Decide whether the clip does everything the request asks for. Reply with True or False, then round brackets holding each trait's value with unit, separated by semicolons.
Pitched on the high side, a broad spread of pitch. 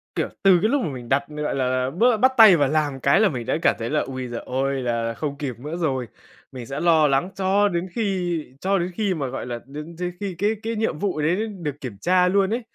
False (155 Hz; 6.1 semitones)